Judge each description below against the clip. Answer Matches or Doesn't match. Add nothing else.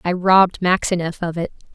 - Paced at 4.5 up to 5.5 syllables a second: Doesn't match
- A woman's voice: Matches